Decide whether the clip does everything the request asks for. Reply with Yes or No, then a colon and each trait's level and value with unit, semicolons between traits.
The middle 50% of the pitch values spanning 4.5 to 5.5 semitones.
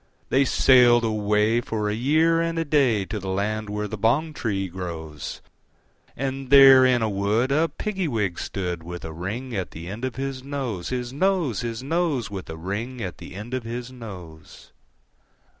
Yes: average, 5.2 semitones